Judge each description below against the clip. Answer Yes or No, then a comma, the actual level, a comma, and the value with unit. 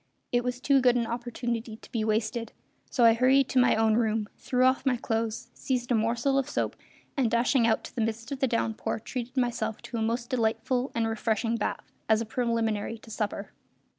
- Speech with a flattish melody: Yes, narrow, 2.0 semitones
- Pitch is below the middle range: No, high, 235 Hz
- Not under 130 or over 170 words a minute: No, fast, 205 wpm